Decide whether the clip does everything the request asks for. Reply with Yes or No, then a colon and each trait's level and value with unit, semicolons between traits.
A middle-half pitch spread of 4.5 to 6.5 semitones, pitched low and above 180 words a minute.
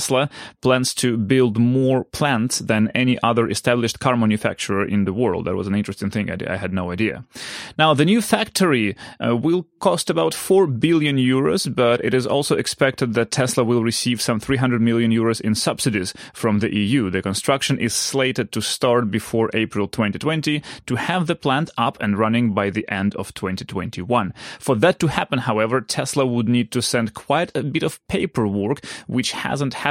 No: average, 3.7 semitones; low, 120 Hz; average, 190 wpm